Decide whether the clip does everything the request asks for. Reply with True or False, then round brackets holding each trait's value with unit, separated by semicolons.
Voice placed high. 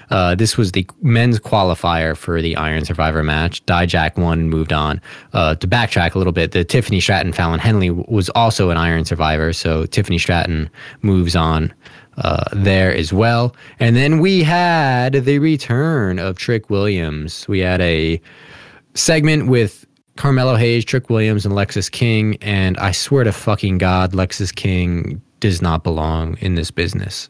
False (95 Hz)